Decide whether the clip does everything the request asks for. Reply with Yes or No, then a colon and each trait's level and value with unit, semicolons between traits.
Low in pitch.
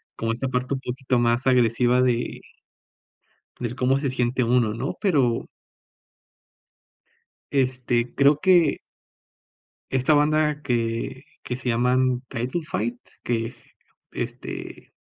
Yes: low, 125 Hz